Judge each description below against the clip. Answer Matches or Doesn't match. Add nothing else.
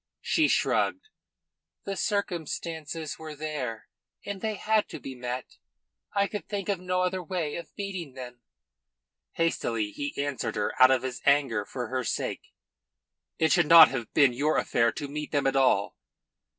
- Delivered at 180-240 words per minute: Doesn't match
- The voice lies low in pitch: Doesn't match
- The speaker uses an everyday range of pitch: Doesn't match